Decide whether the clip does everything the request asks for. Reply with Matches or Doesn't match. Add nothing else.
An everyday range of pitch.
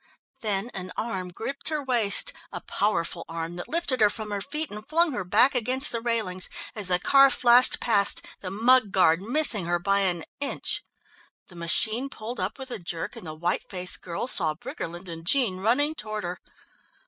Doesn't match